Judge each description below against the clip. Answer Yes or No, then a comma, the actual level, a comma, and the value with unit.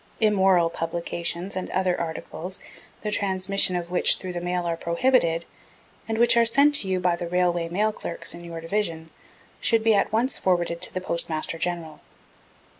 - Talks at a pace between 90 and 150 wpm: No, average, 175 wpm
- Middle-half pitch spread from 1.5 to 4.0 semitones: Yes, average, 3.0 semitones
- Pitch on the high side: No, medium, 180 Hz